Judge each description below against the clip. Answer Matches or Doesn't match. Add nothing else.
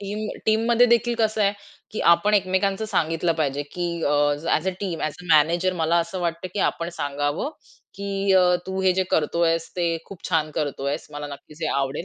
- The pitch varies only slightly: Doesn't match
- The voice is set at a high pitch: Doesn't match